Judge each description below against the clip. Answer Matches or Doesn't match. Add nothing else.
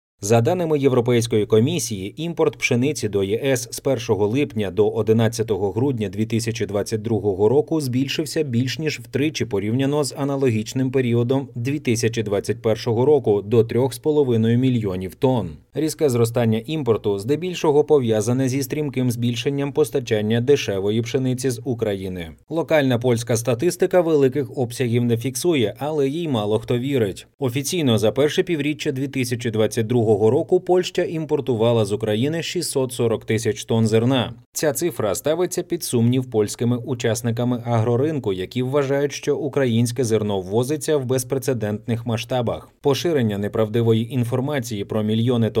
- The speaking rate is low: Doesn't match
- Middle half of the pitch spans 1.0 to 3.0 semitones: Doesn't match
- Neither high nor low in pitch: Doesn't match